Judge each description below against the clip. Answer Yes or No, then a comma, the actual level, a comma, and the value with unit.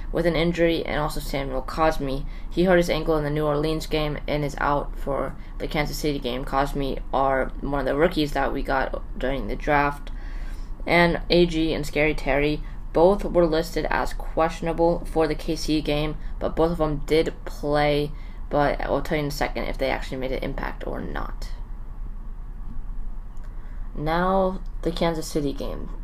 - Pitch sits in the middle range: Yes, medium, 150 Hz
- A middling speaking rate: Yes, average, 175 wpm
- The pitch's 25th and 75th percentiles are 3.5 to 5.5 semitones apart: No, average, 2.9 semitones